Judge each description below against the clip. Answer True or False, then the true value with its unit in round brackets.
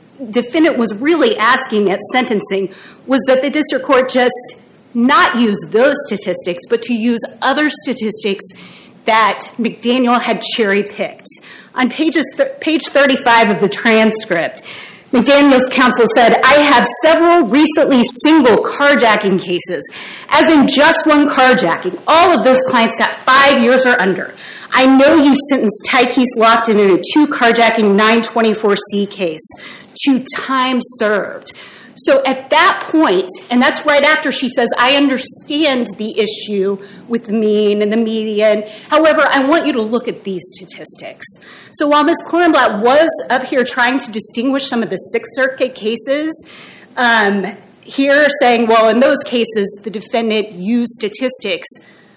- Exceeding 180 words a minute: False (150 wpm)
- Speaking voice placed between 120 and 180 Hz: False (245 Hz)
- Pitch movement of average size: True (4.4 semitones)